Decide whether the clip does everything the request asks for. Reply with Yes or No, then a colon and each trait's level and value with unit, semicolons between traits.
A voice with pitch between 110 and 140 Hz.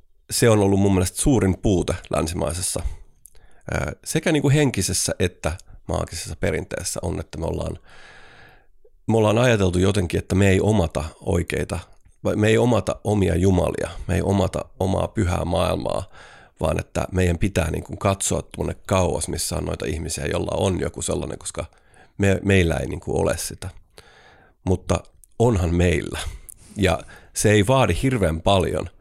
No: very low, 95 Hz